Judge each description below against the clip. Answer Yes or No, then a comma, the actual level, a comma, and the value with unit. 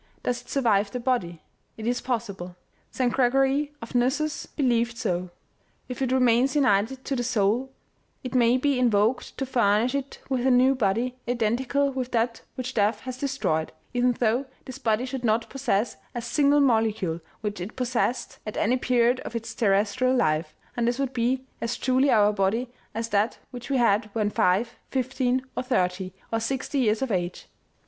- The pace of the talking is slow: No, average, 175 wpm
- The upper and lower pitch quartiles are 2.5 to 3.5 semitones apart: Yes, average, 3.1 semitones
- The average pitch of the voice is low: No, high, 245 Hz